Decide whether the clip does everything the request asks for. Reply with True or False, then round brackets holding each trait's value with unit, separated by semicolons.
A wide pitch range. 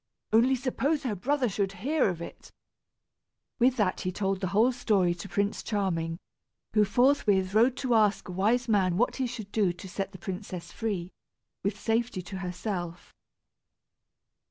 False (4.4 semitones)